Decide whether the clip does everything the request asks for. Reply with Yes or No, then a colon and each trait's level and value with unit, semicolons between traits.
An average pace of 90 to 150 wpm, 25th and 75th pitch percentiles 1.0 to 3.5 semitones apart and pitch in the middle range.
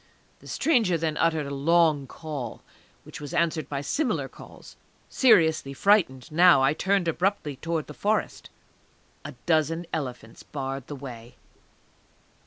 No: slow, 135 wpm; average, 3.9 semitones; medium, 155 Hz